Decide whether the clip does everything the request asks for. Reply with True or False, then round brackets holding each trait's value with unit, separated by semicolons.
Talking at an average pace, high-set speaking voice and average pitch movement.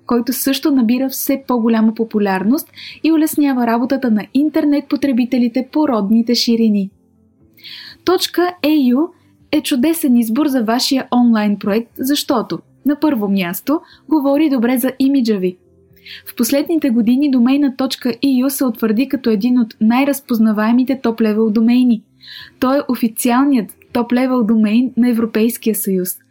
False (125 wpm; 250 Hz; 3.6 semitones)